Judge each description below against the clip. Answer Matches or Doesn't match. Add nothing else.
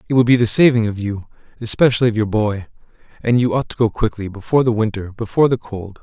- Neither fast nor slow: Doesn't match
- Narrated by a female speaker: Doesn't match